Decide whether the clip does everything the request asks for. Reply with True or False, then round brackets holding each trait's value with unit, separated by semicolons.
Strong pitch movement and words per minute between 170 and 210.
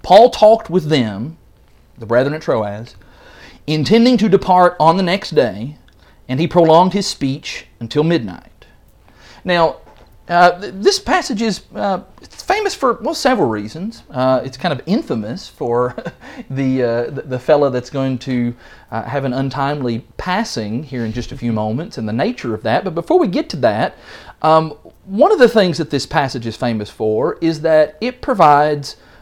True (7.3 semitones; 175 wpm)